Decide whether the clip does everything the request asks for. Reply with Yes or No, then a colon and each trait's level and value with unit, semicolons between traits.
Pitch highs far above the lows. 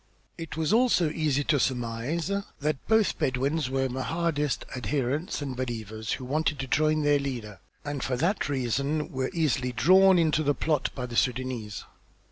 No: average, 3.6 semitones